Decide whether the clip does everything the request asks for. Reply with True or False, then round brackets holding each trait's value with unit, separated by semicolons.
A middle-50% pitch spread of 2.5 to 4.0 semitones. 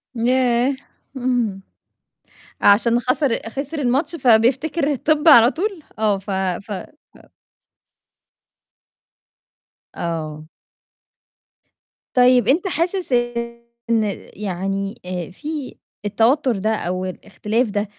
False (5.0 semitones)